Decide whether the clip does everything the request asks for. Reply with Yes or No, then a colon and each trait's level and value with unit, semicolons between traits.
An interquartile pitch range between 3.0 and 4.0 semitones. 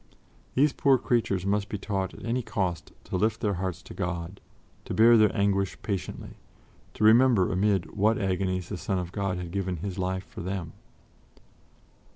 No: narrow, 2.6 semitones